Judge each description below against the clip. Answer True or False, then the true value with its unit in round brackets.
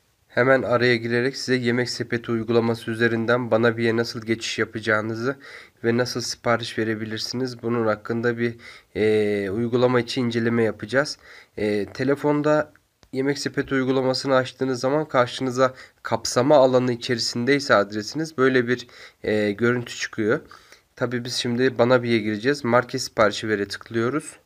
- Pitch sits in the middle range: False (120 Hz)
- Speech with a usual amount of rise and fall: False (2.1 semitones)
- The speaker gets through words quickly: False (130 wpm)